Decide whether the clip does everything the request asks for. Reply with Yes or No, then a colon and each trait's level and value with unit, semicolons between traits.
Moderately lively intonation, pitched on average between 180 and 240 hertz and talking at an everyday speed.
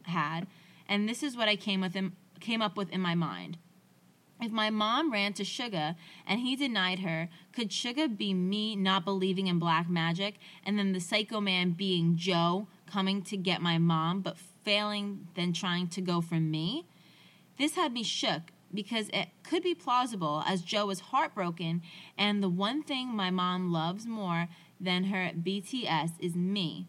Yes: average, 3.1 semitones; high, 190 Hz; average, 180 wpm